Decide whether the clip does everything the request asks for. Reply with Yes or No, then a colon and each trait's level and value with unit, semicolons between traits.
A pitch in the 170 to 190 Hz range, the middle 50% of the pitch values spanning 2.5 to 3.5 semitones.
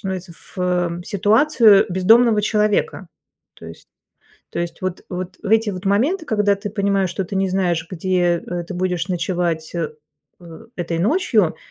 Yes: medium, 185 Hz; average, 2.9 semitones